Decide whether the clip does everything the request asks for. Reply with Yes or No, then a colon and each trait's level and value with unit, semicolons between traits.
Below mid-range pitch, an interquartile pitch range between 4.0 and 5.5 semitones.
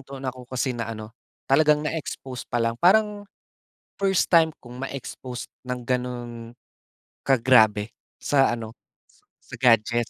No: low, 125 Hz; average, 2.8 semitones